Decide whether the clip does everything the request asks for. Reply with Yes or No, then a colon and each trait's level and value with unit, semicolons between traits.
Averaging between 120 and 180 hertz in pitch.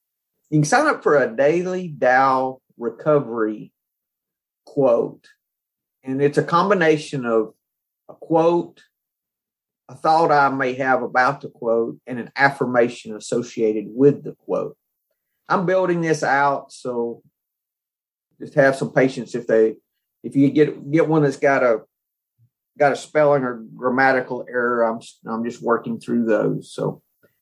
Yes: low, 135 Hz